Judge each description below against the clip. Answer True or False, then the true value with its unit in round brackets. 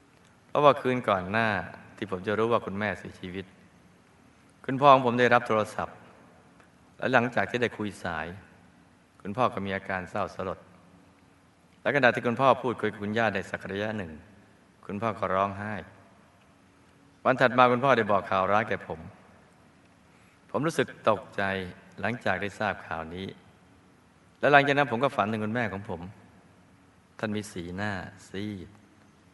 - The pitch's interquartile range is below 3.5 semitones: True (3.1 semitones)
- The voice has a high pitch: False (100 Hz)